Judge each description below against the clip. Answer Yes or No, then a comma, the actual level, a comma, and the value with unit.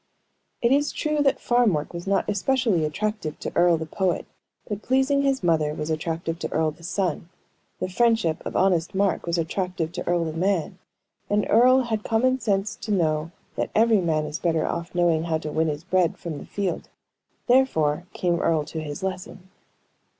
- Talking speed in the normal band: Yes, average, 190 wpm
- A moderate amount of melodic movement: Yes, average, 4.9 semitones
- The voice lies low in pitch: No, medium, 180 Hz